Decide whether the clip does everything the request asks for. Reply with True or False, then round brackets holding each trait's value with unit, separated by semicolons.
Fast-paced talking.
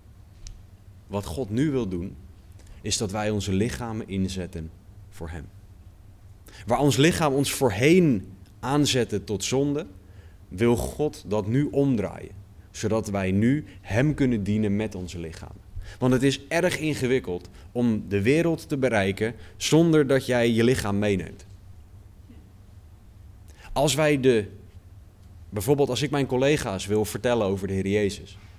False (135 wpm)